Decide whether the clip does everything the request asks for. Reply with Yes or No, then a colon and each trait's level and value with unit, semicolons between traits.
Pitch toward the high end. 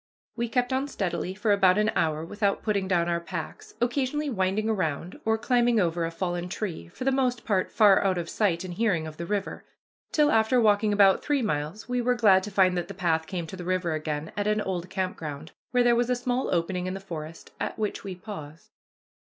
Yes: high, 195 Hz